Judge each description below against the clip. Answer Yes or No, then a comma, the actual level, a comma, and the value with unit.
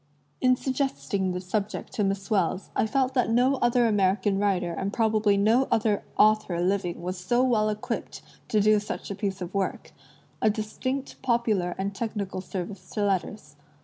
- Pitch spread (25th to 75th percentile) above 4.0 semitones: No, average, 3.1 semitones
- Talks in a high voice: Yes, high, 205 Hz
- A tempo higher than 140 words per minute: Yes, average, 175 wpm